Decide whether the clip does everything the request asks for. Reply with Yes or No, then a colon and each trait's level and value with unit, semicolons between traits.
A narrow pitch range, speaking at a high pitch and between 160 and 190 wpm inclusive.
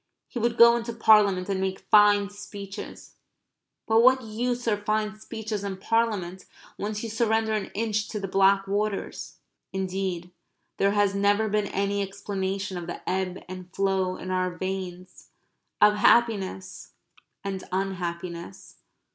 No: narrow, 2.3 semitones; high, 200 Hz; average, 140 wpm